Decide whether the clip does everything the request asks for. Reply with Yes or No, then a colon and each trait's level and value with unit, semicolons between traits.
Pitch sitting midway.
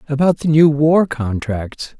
Yes: medium, 145 Hz